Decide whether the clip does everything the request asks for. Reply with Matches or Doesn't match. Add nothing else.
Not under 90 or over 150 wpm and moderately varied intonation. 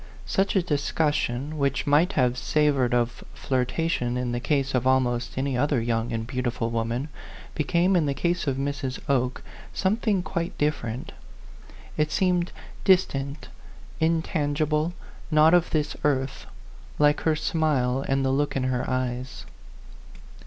Matches